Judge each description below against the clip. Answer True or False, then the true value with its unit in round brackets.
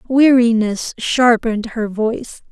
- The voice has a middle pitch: False (230 Hz)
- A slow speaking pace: True (95 wpm)